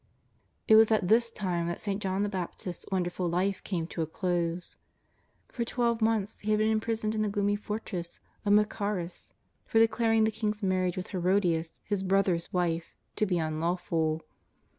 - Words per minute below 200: Yes, average, 175 wpm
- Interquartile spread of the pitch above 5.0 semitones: No, average, 3.5 semitones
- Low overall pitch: No, high, 195 Hz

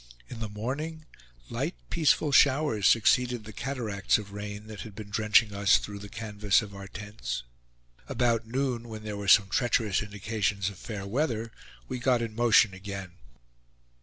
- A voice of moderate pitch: No, low, 110 Hz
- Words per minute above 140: Yes, average, 165 wpm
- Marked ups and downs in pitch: No, average, 2.8 semitones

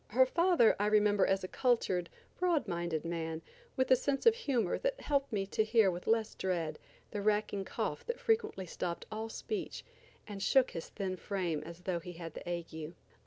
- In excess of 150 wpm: Yes, average, 190 wpm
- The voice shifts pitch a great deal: Yes, wide, 6.7 semitones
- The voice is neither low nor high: No, high, 200 Hz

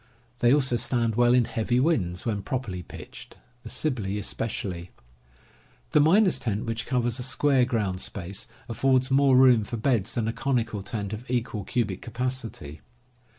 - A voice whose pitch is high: No, low, 120 Hz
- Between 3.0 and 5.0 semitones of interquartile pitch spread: Yes, average, 3.8 semitones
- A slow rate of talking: No, average, 155 wpm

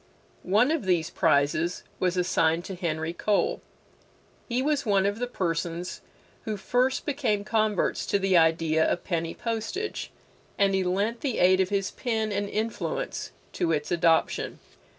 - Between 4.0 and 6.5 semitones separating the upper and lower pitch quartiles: Yes, average, 4.8 semitones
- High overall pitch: Yes, high, 195 Hz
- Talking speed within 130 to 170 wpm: Yes, average, 150 wpm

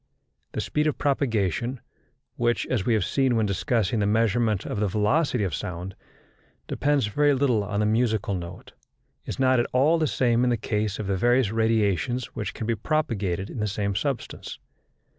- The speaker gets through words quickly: No, average, 180 wpm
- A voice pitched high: No, low, 110 Hz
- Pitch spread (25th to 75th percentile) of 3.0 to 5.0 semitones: Yes, average, 4.0 semitones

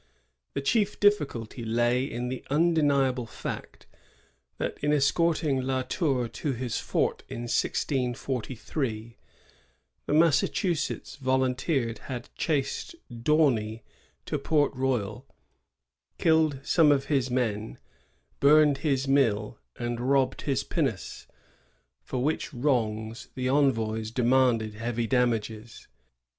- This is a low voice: Yes, low, 130 Hz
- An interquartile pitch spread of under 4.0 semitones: Yes, average, 3.5 semitones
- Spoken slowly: Yes, slow, 105 wpm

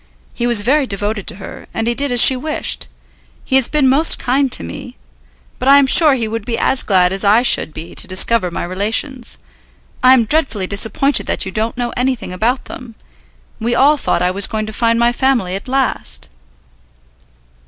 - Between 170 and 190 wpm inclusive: No, average, 200 wpm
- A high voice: Yes, high, 235 Hz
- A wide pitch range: No, average, 4.6 semitones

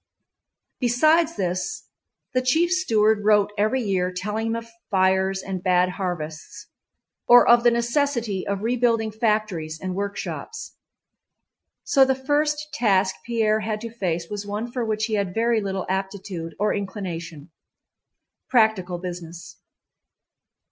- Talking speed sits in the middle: No, slow, 125 wpm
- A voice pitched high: Yes, high, 210 Hz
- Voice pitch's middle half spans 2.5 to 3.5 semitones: No, average, 4.1 semitones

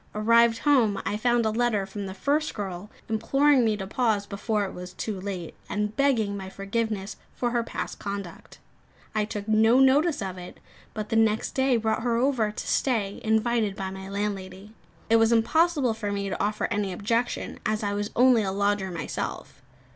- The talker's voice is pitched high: Yes, high, 215 Hz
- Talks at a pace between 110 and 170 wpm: No, average, 185 wpm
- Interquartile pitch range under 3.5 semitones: Yes, average, 2.8 semitones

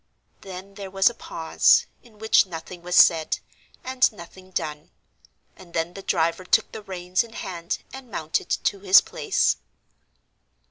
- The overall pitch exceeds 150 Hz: Yes, medium, 185 Hz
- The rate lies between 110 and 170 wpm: Yes, average, 150 wpm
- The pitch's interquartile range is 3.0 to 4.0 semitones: Yes, average, 3.3 semitones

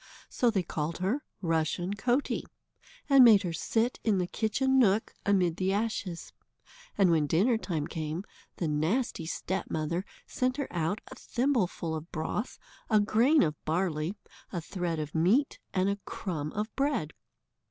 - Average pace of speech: Yes, average, 155 wpm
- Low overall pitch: No, high, 190 Hz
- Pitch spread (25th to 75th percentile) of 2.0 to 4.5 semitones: No, wide, 5.4 semitones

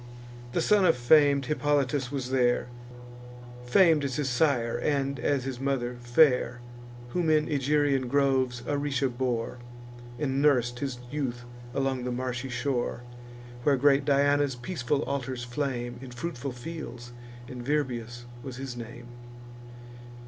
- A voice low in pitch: Yes, low, 130 Hz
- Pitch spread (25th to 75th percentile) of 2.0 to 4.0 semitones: Yes, average, 2.8 semitones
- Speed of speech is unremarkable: No, slow, 130 wpm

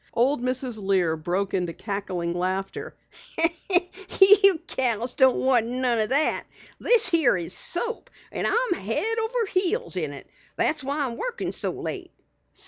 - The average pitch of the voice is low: No, very high, 255 Hz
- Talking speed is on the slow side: No, average, 145 wpm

